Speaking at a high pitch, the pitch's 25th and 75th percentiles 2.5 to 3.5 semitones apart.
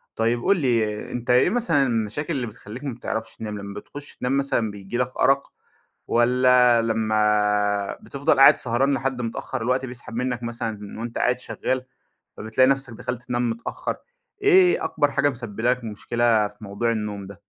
No: low, 120 Hz; average, 3.0 semitones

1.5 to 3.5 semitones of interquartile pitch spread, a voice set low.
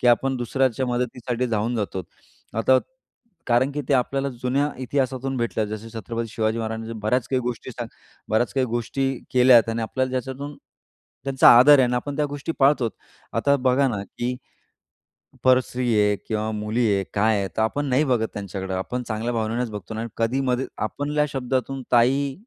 Yes: average, 3.0 semitones; low, 125 Hz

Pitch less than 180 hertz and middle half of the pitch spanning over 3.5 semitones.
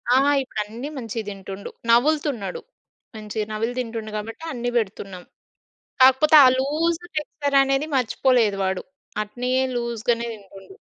No: high, 235 Hz; average, 4.0 semitones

